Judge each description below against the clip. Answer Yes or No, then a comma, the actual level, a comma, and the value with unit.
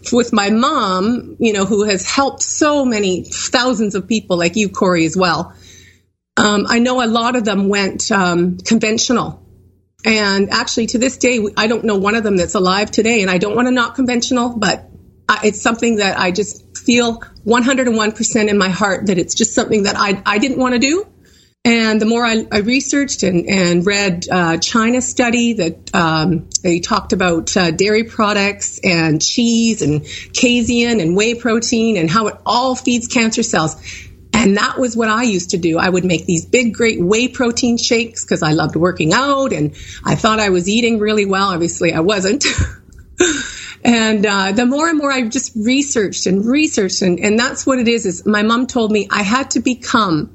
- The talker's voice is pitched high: Yes, high, 215 Hz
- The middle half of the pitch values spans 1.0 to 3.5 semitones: No, average, 4.5 semitones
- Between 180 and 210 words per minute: Yes, average, 195 wpm